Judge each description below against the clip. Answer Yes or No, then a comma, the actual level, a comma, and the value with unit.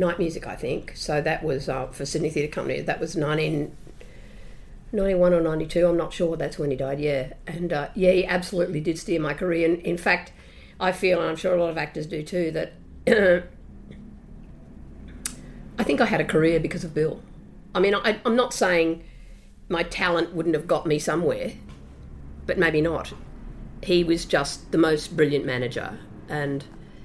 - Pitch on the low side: No, medium, 165 Hz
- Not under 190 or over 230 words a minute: No, average, 180 wpm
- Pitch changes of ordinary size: Yes, average, 3.3 semitones